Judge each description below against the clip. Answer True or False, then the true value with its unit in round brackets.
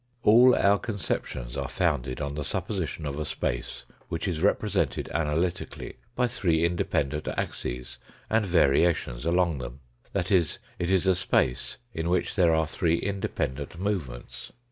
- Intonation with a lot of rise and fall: False (4.9 semitones)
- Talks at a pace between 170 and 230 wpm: False (150 wpm)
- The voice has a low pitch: True (85 Hz)